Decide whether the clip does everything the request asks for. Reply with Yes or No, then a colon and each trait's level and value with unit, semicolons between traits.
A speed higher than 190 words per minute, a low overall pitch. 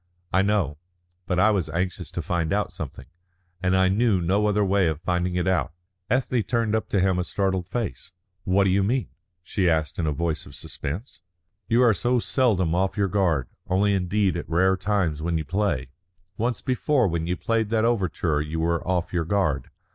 Yes: average, 200 wpm; very low, 95 Hz